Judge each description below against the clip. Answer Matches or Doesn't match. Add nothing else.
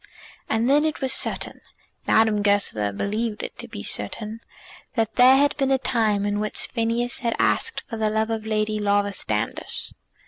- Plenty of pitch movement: Doesn't match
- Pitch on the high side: Matches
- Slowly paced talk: Doesn't match